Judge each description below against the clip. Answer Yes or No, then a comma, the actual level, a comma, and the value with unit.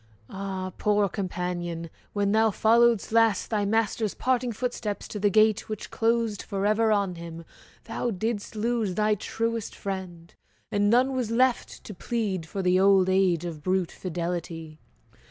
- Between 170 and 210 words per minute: No, average, 150 wpm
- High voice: Yes, high, 205 Hz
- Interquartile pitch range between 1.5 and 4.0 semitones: Yes, average, 3.6 semitones